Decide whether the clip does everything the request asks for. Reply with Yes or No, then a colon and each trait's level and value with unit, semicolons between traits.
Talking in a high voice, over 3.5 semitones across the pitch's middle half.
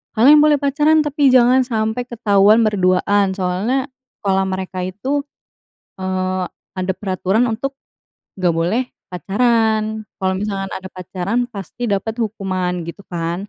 Yes: high, 205 Hz; average, 4.4 semitones